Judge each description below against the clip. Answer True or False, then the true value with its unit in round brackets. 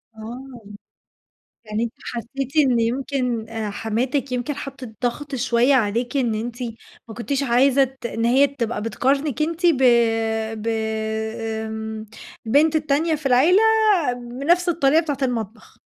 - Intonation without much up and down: False (3.5 semitones)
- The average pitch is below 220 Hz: False (250 Hz)